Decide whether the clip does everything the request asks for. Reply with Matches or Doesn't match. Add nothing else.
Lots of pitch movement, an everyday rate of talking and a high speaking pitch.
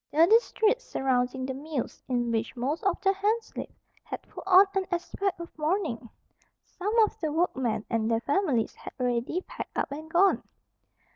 Matches